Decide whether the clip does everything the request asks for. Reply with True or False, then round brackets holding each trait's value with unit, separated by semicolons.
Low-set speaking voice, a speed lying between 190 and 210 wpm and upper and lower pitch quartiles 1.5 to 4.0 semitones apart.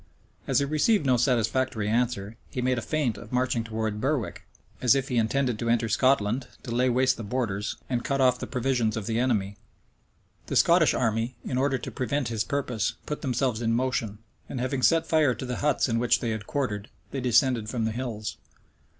True (125 Hz; 200 wpm; 2.6 semitones)